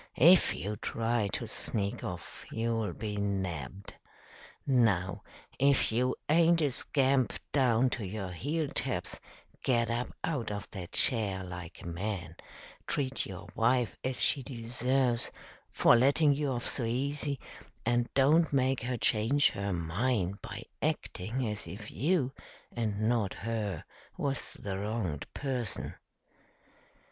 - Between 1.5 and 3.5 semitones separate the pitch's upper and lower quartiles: No, average, 4.7 semitones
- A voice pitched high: No, low, 115 Hz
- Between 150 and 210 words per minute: No, slow, 135 wpm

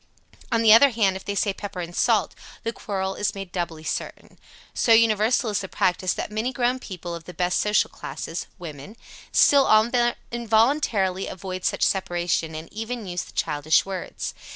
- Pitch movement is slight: No, average, 4.2 semitones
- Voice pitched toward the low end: No, high, 195 Hz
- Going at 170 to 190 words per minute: Yes, average, 175 wpm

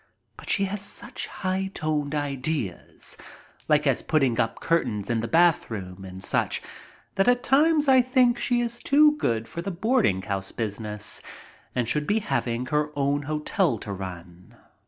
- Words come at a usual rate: Yes, average, 160 wpm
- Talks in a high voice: No, medium, 150 Hz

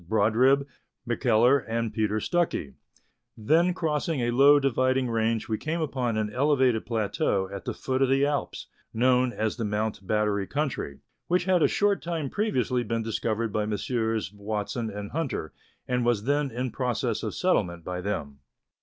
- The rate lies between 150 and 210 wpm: Yes, average, 165 wpm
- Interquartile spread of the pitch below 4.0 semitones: No, average, 4.3 semitones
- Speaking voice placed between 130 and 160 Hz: No, low, 120 Hz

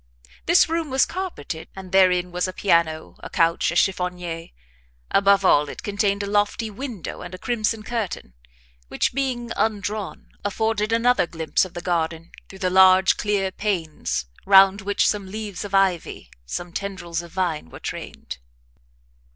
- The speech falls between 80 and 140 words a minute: No, average, 155 wpm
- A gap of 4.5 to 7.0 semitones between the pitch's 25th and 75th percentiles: No, average, 3.2 semitones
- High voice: Yes, high, 195 Hz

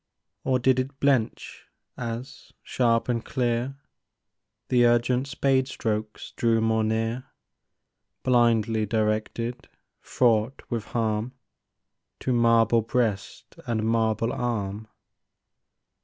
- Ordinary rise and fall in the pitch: No, narrow, 2.0 semitones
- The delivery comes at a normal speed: No, slow, 95 wpm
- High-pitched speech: No, low, 115 Hz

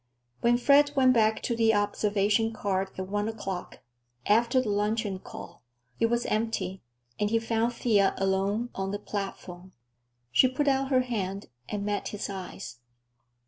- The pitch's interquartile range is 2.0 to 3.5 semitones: Yes, average, 3.2 semitones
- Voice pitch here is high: Yes, high, 210 Hz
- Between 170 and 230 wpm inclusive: No, average, 155 wpm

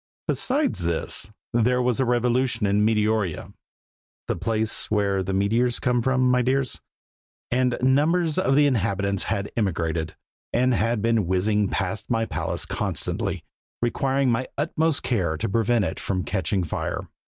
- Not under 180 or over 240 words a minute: No, average, 145 wpm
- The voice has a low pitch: Yes, low, 115 Hz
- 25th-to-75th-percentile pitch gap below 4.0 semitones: No, average, 4.3 semitones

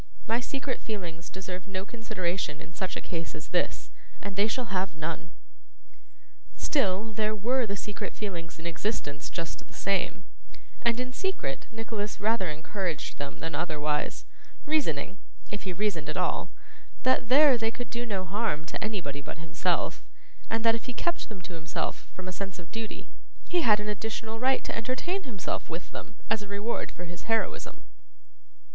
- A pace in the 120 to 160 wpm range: No, average, 175 wpm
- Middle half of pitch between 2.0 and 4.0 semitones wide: No, average, 4.6 semitones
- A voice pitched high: Yes, high, 200 Hz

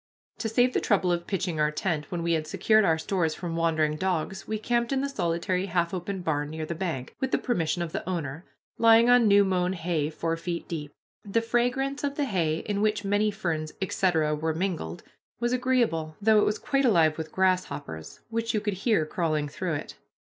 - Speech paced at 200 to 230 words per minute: Yes, fast, 205 wpm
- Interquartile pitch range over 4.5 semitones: Yes, average, 5.2 semitones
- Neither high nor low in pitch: Yes, medium, 180 Hz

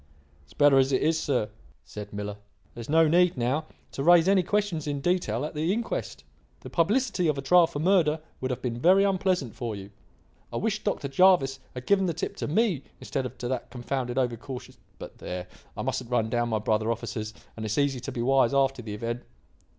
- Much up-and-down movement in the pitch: Yes, wide, 6.4 semitones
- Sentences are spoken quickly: Yes, fast, 215 wpm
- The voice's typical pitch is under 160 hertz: Yes, low, 135 Hz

